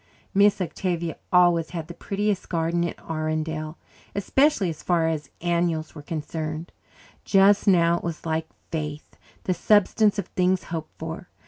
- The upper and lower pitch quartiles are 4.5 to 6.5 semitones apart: No, narrow, 2.6 semitones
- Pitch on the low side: No, medium, 170 Hz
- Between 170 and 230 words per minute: No, average, 145 wpm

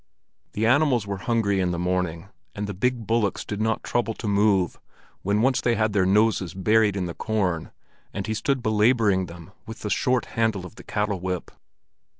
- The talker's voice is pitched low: Yes, low, 105 Hz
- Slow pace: No, average, 190 wpm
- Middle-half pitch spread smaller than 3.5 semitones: Yes, average, 3.1 semitones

